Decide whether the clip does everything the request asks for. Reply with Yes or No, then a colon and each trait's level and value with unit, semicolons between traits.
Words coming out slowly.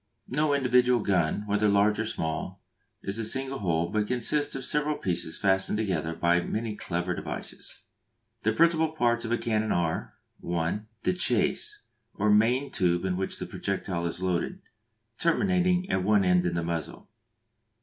No: average, 160 wpm